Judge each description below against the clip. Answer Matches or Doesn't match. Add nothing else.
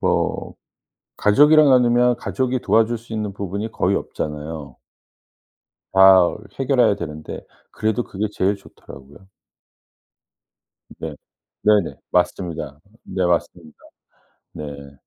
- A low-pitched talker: Matches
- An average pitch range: Doesn't match